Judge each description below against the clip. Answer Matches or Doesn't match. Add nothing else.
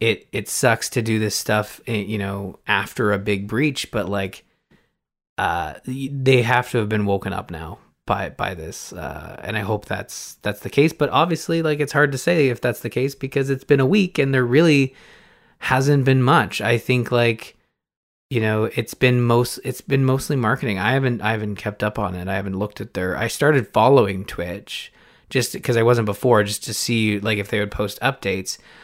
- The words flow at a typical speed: Doesn't match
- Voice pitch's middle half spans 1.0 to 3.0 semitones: Doesn't match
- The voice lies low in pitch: Matches